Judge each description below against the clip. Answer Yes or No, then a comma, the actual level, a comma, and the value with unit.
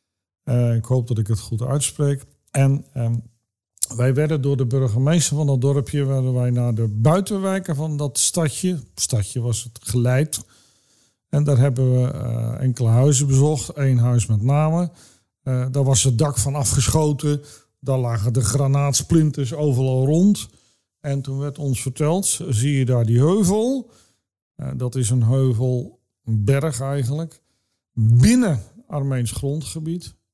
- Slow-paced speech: No, average, 150 wpm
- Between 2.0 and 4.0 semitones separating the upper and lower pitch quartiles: Yes, average, 3.6 semitones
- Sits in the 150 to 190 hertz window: No, low, 135 Hz